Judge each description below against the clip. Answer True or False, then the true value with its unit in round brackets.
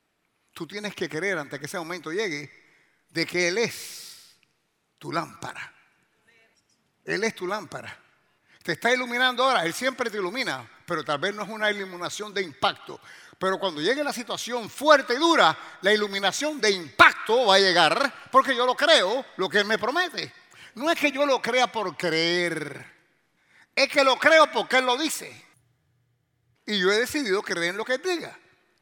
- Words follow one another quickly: False (180 wpm)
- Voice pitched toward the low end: False (210 Hz)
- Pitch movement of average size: False (7.2 semitones)